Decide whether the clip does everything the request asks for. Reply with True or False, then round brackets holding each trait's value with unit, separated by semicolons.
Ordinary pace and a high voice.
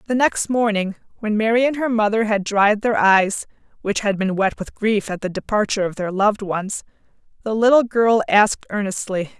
True (190 wpm; 210 Hz)